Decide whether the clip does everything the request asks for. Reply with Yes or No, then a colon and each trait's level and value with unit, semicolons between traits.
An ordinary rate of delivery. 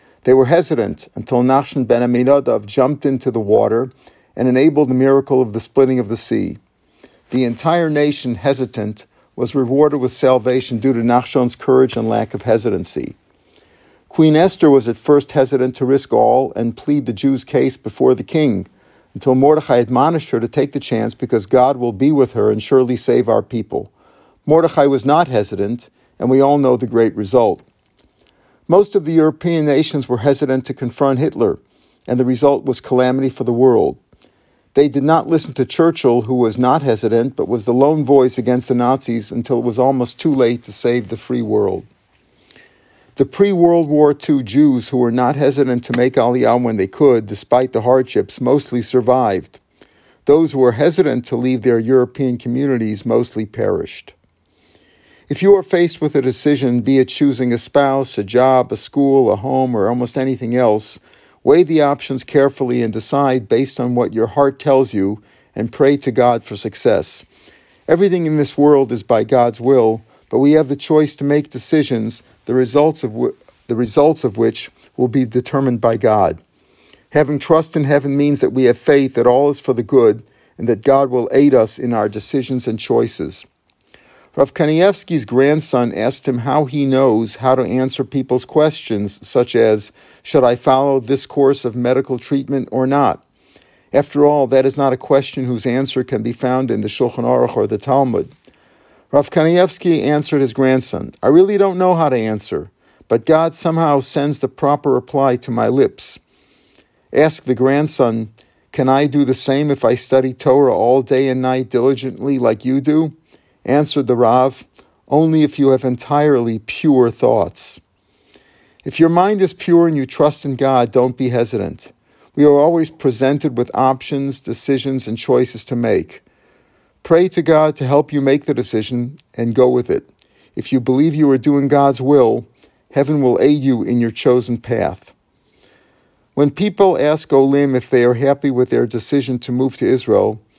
Yes: average, 180 wpm